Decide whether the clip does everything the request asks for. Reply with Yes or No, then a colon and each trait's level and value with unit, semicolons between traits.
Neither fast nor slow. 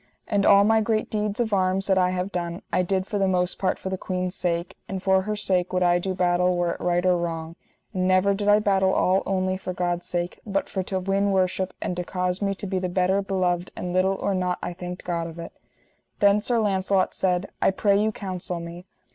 No: fast, 240 wpm